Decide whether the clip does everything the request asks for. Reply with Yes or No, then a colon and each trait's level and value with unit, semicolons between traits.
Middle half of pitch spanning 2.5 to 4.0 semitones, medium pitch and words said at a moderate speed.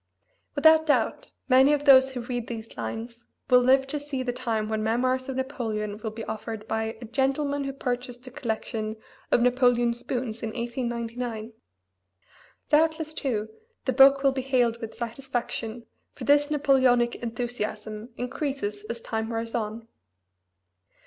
No: average, 2.9 semitones; high, 245 Hz; average, 150 wpm